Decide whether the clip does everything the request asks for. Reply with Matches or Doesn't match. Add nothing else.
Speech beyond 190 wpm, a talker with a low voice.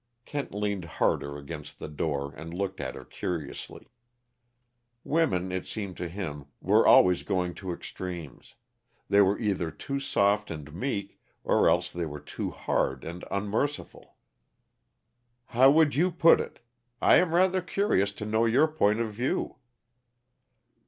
Doesn't match